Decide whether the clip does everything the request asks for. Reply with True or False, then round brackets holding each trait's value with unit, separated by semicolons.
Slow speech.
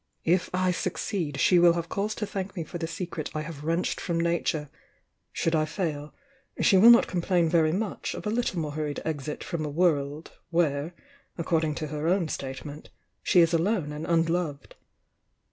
False (185 wpm)